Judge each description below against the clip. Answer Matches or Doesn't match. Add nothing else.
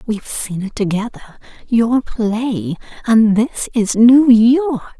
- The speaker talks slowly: Matches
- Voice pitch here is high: Matches